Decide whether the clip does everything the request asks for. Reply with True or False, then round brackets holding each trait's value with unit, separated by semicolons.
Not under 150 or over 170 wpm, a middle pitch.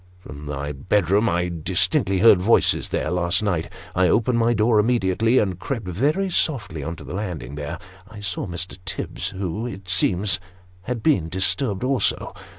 False (165 wpm; 95 Hz)